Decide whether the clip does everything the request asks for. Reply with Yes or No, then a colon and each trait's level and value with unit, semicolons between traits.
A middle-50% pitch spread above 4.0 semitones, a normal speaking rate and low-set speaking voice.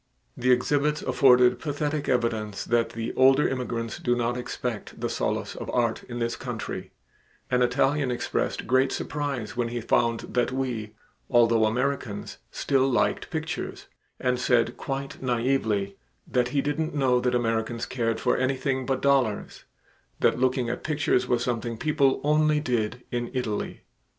No: narrow, 2.5 semitones; average, 150 wpm; low, 125 Hz